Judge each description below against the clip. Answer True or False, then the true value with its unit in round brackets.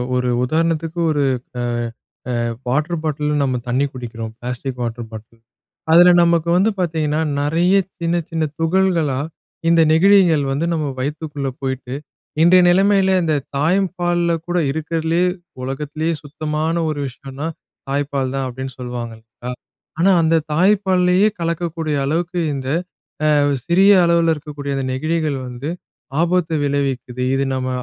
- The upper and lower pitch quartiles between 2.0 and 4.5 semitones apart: True (4.1 semitones)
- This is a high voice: False (155 Hz)